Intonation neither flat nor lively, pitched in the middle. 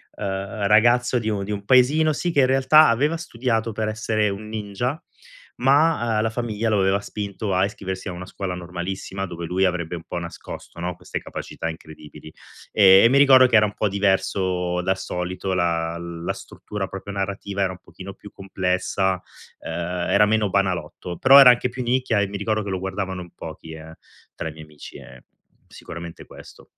No: average, 3.7 semitones; low, 100 Hz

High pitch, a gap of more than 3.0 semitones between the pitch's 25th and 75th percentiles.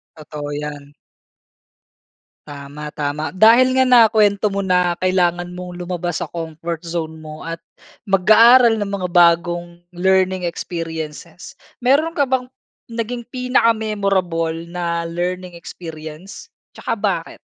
No: medium, 175 Hz; average, 4.1 semitones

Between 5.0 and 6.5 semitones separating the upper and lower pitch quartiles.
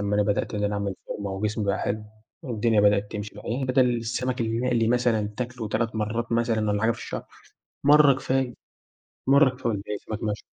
No: average, 3.0 semitones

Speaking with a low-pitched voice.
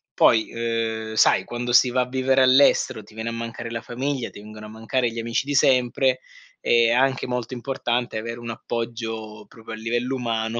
Yes: low, 115 Hz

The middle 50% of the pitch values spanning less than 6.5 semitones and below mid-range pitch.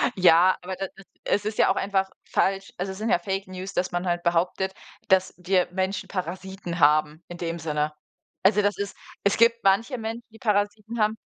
No: narrow, 2.6 semitones; high, 190 Hz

